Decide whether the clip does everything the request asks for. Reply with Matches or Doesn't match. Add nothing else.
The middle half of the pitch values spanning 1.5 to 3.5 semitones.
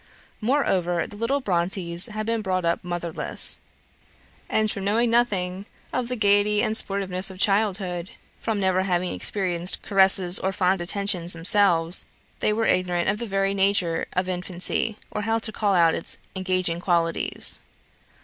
Matches